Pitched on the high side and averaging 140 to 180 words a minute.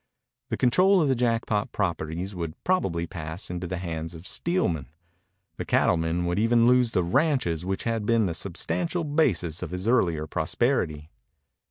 No: very low, 95 Hz; average, 160 wpm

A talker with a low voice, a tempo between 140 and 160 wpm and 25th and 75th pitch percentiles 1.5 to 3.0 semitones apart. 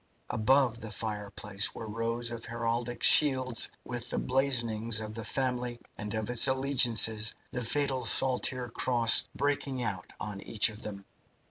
Yes: low, 115 Hz; average, 145 wpm; average, 2.7 semitones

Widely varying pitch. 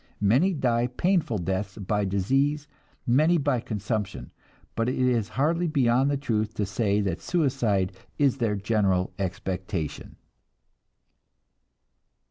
Yes: wide, 5.7 semitones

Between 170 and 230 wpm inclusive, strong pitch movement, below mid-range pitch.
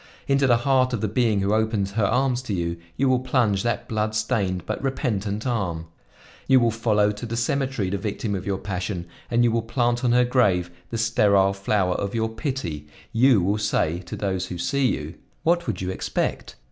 No: fast, 205 wpm; average, 4.0 semitones; low, 110 Hz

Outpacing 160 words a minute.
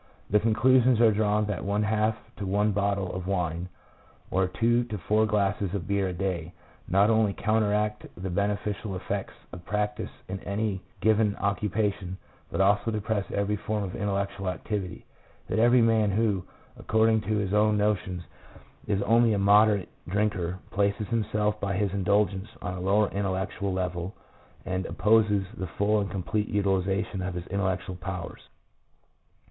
No: average, 155 wpm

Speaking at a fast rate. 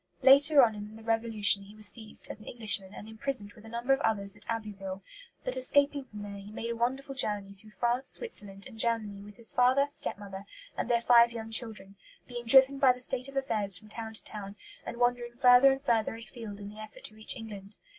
Yes: fast, 225 wpm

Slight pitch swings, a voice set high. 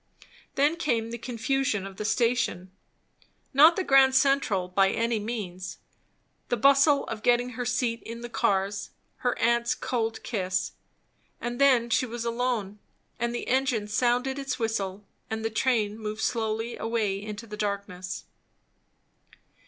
No: average, 3.1 semitones; high, 230 Hz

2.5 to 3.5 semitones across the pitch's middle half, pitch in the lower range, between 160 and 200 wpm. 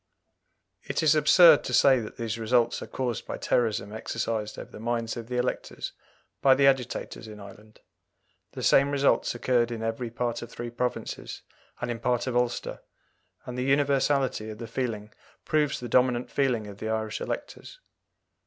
Yes: average, 2.8 semitones; low, 120 Hz; average, 170 wpm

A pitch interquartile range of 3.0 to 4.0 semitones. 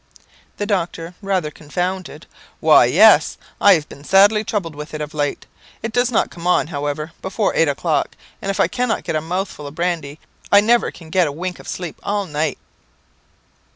No: average, 4.5 semitones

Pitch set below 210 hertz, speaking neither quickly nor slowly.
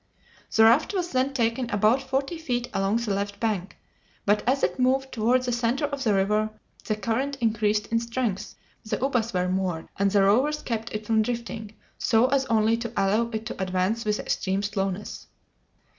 No: high, 225 Hz; average, 185 wpm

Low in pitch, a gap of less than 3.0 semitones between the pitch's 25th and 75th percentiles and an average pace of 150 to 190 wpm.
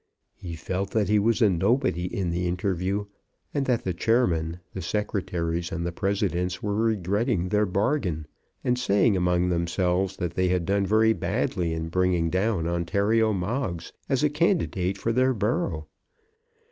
No: very low, 95 Hz; average, 3.9 semitones; average, 160 wpm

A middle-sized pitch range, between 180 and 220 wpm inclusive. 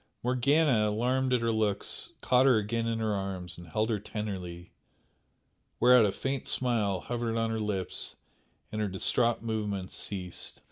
No: average, 3.3 semitones; average, 155 wpm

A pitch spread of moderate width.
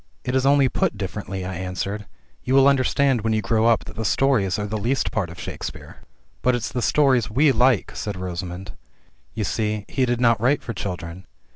Yes: average, 4.8 semitones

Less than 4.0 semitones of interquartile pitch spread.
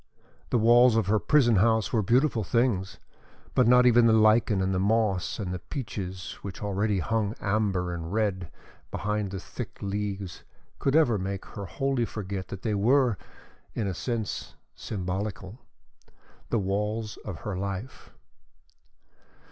Yes: average, 3.1 semitones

